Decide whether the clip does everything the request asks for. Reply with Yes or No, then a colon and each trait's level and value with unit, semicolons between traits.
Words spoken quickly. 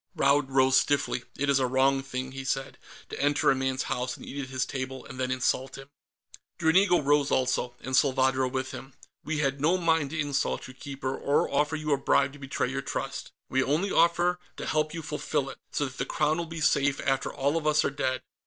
Yes: fast, 225 wpm